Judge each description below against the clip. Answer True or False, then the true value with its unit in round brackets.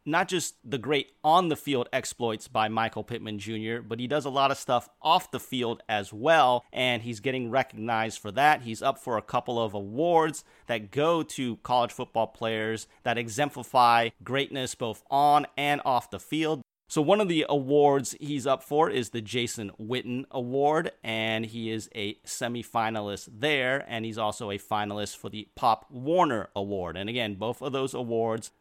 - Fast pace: False (180 wpm)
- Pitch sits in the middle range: False (120 Hz)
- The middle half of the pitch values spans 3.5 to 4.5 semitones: True (3.8 semitones)